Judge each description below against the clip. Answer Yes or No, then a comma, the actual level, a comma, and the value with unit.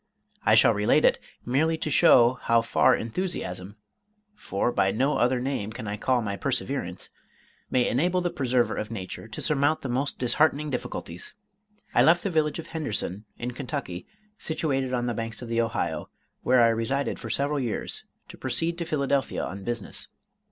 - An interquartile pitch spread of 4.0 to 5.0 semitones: Yes, average, 4.3 semitones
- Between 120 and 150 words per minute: No, average, 175 wpm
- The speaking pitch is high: No, low, 125 Hz